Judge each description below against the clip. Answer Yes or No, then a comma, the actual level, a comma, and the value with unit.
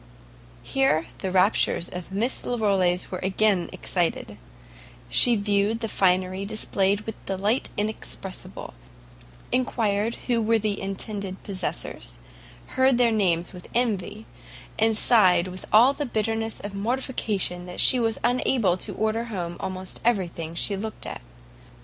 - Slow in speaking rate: Yes, slow, 130 wpm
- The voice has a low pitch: No, high, 205 Hz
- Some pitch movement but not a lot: Yes, average, 3.3 semitones